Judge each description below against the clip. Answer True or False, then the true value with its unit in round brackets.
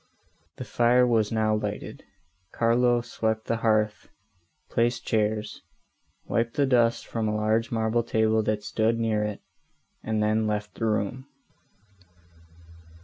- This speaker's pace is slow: True (130 wpm)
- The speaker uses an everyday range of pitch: False (1.5 semitones)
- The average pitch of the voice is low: True (110 Hz)